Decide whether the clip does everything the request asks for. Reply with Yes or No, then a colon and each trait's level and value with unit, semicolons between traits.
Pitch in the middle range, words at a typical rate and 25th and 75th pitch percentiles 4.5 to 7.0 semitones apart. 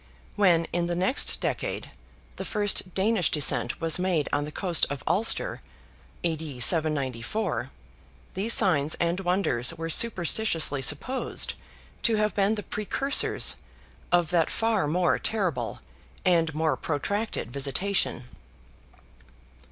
No: medium, 175 Hz; slow, 120 wpm; average, 5.0 semitones